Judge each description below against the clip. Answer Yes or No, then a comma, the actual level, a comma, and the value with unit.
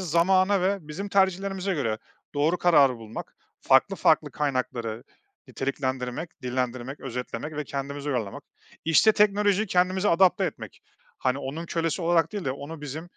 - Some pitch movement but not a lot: No, wide, 5.9 semitones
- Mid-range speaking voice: Yes, medium, 155 Hz